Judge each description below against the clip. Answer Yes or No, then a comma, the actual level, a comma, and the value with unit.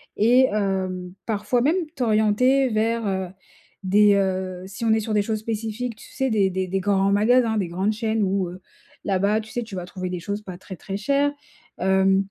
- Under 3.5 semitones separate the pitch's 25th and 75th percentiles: Yes, average, 2.7 semitones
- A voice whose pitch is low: No, high, 205 Hz